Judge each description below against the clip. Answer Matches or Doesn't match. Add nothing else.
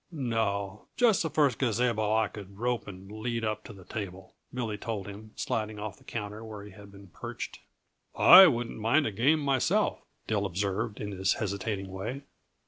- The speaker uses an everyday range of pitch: Matches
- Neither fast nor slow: Matches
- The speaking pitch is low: Matches